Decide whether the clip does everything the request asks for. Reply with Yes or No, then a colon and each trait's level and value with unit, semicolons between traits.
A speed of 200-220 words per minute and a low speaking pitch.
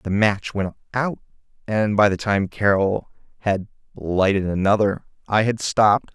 No: average, 145 wpm; low, 100 Hz